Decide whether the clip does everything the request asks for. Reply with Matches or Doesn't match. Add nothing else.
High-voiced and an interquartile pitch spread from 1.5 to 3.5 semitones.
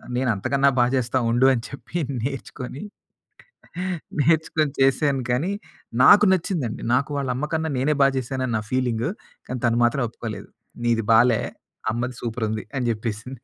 Doesn't match